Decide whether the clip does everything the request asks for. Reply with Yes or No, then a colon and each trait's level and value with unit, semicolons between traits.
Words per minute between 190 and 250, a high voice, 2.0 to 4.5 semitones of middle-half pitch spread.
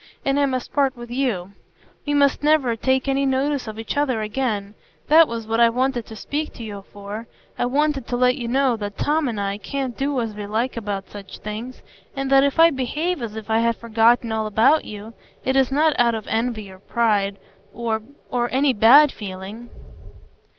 Yes: average, 200 wpm; high, 240 Hz; average, 3.9 semitones